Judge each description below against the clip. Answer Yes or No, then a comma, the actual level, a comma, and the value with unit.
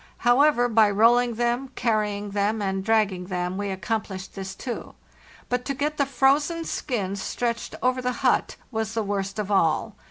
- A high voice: Yes, high, 220 Hz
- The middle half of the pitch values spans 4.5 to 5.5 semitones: No, average, 3.8 semitones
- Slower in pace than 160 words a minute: No, average, 165 wpm